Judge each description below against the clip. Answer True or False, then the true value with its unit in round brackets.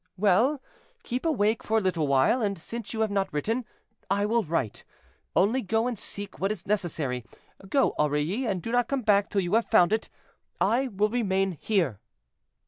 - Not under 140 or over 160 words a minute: False (185 wpm)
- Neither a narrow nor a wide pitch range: True (4.1 semitones)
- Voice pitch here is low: False (205 Hz)